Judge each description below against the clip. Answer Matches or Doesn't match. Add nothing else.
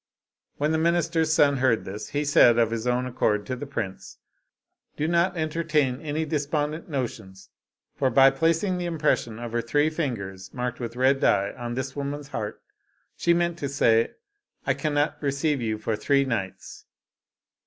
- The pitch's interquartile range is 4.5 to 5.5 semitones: Matches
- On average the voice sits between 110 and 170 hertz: Matches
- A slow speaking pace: Doesn't match